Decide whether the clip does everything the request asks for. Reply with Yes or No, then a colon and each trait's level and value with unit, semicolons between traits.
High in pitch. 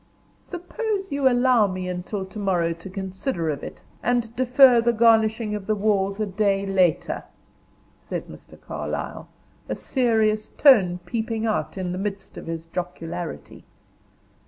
Yes: high, 210 Hz